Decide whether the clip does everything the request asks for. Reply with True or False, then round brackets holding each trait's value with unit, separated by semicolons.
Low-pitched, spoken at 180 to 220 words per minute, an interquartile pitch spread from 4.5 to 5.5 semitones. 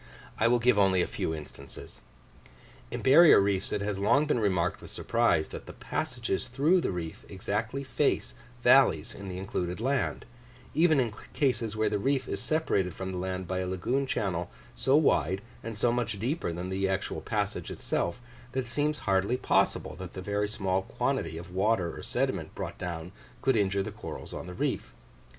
True (100 Hz; 185 wpm; 4.9 semitones)